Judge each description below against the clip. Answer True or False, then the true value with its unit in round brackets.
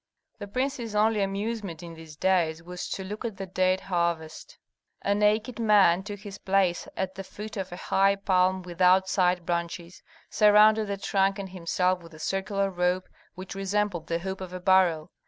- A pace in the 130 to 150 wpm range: False (180 wpm)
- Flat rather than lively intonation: True (2.3 semitones)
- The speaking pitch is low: False (190 Hz)